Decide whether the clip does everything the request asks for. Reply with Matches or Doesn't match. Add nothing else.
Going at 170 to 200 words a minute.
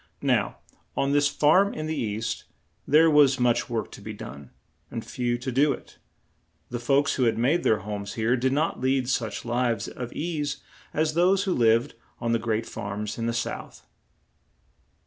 Matches